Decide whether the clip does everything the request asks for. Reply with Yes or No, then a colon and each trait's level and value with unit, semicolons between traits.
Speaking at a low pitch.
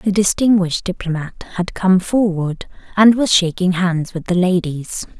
No: medium, 185 Hz